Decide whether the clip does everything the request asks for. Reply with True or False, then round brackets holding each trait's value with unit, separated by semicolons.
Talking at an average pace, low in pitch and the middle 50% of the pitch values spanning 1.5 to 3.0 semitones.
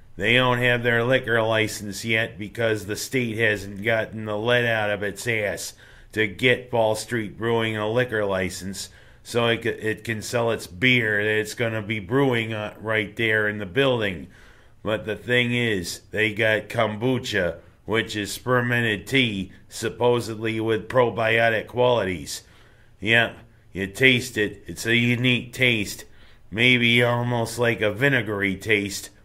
True (150 wpm; 110 Hz; 2.4 semitones)